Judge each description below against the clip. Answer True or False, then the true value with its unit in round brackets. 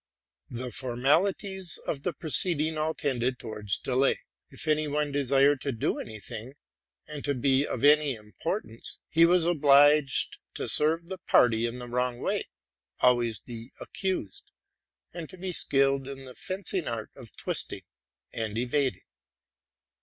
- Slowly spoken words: False (150 wpm)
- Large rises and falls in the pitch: False (4.2 semitones)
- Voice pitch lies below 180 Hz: True (140 Hz)